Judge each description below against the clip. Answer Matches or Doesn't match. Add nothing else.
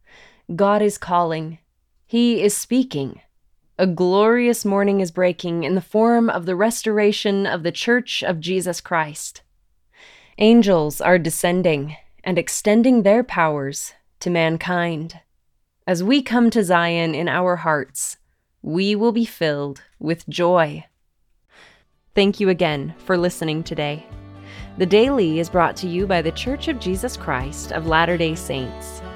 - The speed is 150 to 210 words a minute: Doesn't match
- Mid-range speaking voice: Matches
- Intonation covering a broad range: Doesn't match